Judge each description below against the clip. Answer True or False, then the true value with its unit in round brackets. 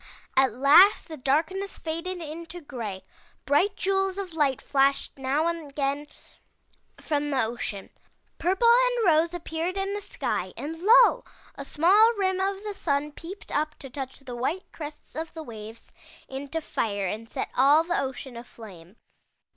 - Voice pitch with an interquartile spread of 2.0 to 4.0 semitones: False (5.5 semitones)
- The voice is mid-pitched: False (305 Hz)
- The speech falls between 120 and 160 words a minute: True (155 wpm)